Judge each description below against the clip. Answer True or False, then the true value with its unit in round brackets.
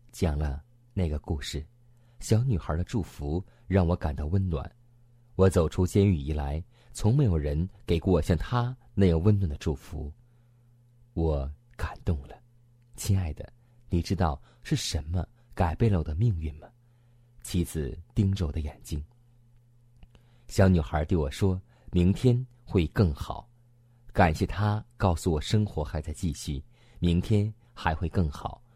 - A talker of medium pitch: False (95 Hz)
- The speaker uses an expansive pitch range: True (6.8 semitones)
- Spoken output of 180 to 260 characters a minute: True (205 characters per minute)